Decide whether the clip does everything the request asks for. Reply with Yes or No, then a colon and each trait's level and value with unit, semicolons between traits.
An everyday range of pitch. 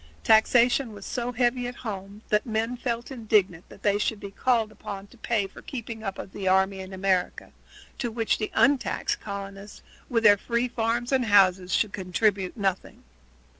Yes: average, 3.3 semitones